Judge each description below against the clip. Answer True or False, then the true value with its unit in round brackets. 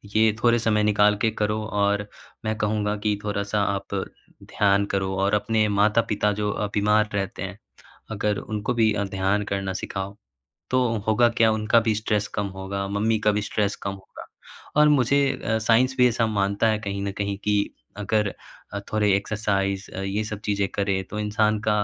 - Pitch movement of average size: False (1.5 semitones)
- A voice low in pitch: True (105 Hz)